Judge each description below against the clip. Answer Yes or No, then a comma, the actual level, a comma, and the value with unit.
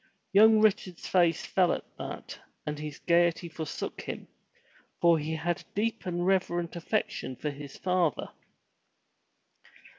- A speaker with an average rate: No, slow, 130 wpm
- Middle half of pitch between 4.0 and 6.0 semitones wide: No, average, 2.8 semitones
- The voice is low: No, medium, 175 Hz